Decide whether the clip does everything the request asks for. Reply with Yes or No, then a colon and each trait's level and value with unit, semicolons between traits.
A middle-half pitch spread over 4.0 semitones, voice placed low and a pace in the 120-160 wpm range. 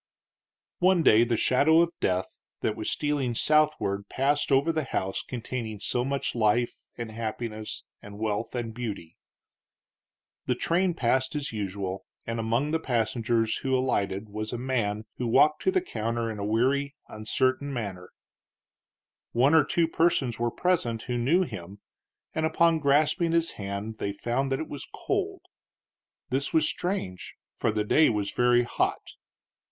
Yes: average, 5.2 semitones; low, 120 Hz; average, 155 wpm